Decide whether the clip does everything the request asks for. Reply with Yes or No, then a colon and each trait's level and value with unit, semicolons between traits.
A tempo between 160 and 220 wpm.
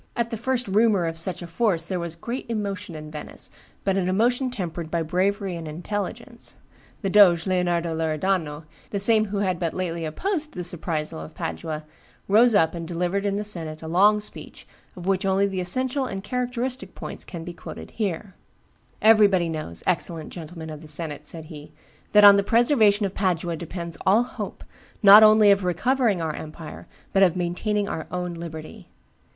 Yes: average, 180 wpm